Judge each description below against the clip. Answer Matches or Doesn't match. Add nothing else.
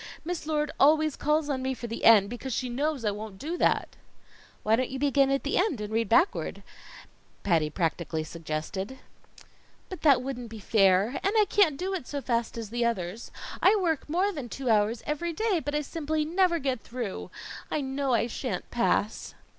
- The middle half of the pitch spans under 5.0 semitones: Doesn't match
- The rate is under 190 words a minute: Doesn't match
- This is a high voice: Matches